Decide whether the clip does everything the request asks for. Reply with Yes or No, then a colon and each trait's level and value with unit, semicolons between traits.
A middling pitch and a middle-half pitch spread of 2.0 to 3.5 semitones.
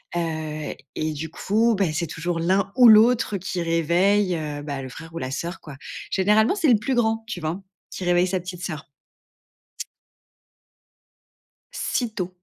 No: medium, 175 Hz; average, 4.6 semitones